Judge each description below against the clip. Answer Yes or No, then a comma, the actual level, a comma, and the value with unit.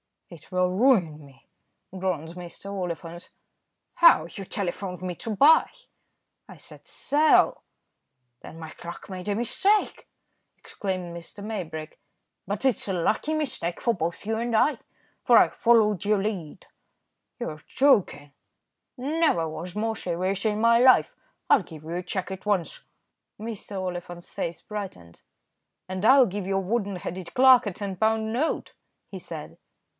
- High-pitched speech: Yes, high, 195 Hz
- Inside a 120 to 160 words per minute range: Yes, average, 140 wpm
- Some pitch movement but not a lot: Yes, average, 4.3 semitones